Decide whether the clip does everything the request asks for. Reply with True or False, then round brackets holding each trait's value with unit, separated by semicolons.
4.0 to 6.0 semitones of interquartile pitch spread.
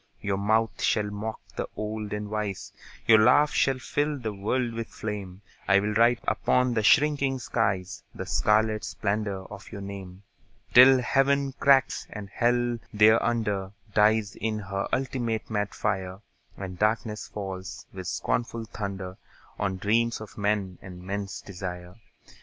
False (2.9 semitones)